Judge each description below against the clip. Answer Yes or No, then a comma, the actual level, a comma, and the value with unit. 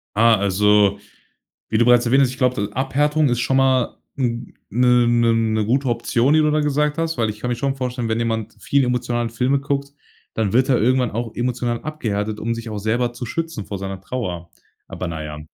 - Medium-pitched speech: No, low, 120 Hz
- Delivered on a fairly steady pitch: No, average, 3.2 semitones